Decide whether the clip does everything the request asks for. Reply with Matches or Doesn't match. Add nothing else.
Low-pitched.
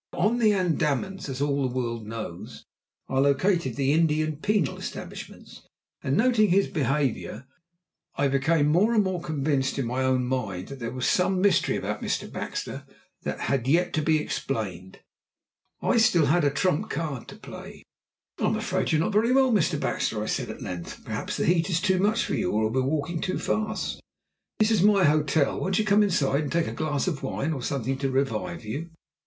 Doesn't match